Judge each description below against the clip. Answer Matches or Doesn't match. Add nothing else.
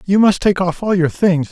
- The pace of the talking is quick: Matches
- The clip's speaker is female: Doesn't match